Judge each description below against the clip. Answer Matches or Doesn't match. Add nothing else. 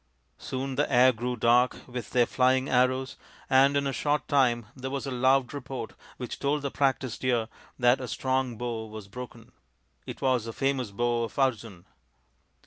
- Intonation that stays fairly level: Matches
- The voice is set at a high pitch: Doesn't match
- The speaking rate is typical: Matches